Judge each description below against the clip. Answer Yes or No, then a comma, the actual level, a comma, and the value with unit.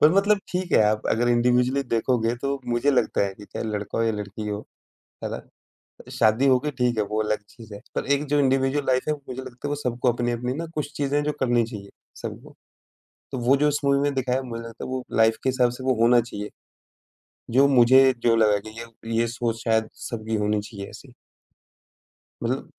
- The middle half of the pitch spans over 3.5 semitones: No, average, 3.2 semitones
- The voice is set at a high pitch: No, low, 120 Hz